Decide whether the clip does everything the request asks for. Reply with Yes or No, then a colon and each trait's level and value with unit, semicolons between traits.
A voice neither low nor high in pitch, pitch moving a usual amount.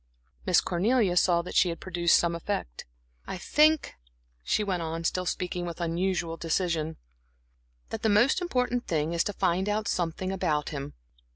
Yes: medium, 175 Hz; average, 3.4 semitones